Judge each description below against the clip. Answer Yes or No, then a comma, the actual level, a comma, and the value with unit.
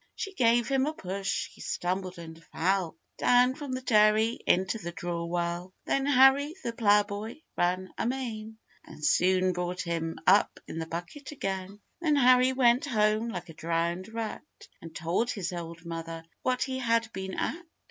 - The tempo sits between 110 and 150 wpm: No, average, 165 wpm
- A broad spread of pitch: Yes, wide, 6.0 semitones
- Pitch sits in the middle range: No, high, 200 Hz